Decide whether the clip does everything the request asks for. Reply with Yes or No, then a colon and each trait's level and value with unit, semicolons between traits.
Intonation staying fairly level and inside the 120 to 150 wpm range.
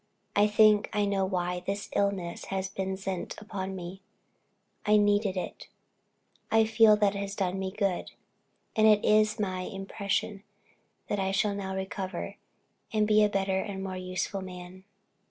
No: narrow, 1.6 semitones; average, 160 wpm